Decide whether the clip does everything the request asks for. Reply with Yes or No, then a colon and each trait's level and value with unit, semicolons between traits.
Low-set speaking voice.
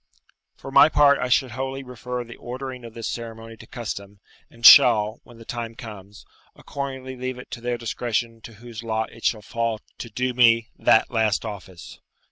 Yes: low, 115 Hz